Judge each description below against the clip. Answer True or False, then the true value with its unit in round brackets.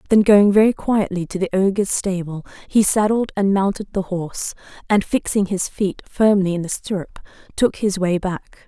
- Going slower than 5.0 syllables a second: True (4.8 syllables/s)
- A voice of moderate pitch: False (195 Hz)